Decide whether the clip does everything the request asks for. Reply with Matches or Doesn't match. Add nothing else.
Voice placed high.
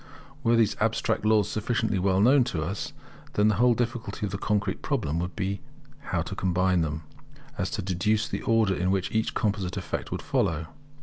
Doesn't match